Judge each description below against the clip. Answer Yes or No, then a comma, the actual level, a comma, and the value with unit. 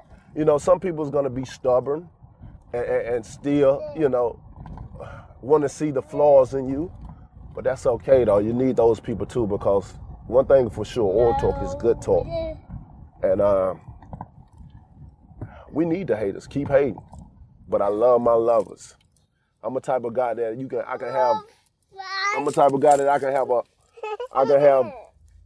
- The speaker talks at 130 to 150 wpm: No, average, 175 wpm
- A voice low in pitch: No, medium, 145 Hz